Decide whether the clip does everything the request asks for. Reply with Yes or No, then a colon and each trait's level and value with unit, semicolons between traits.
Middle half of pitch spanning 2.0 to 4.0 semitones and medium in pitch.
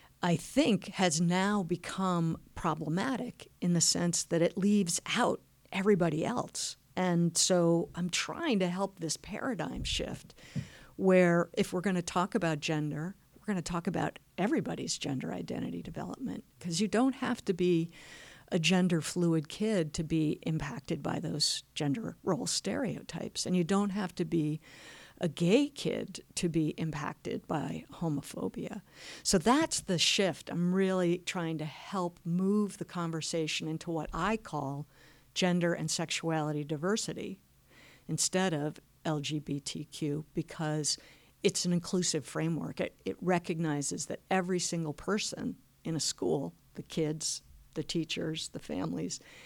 Yes: average, 3.0 semitones; medium, 170 Hz